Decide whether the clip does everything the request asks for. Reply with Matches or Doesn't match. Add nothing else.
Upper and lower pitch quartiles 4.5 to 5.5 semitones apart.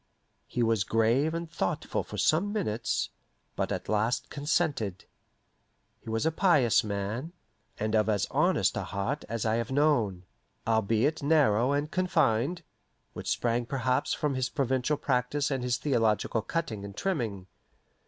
Matches